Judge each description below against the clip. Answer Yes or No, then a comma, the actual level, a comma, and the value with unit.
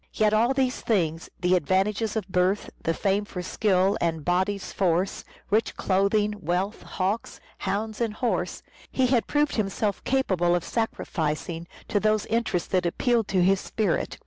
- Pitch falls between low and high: No, high, 200 Hz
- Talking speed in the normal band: Yes, average, 155 wpm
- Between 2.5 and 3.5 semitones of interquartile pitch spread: Yes, average, 3.2 semitones